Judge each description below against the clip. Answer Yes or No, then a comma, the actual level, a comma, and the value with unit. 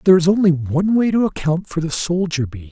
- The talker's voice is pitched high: No, medium, 170 Hz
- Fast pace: Yes, fast, 245 wpm